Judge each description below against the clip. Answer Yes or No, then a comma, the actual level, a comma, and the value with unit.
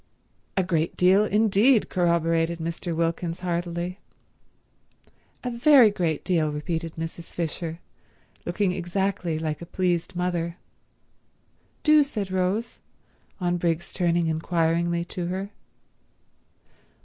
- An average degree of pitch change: No, narrow, 2.3 semitones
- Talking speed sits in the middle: No, slow, 105 wpm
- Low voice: No, medium, 175 Hz